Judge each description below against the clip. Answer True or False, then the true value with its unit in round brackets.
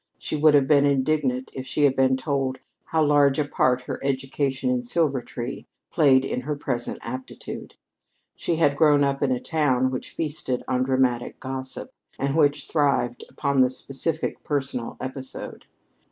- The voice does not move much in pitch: True (2.1 semitones)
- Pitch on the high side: False (135 Hz)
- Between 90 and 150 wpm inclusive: False (160 wpm)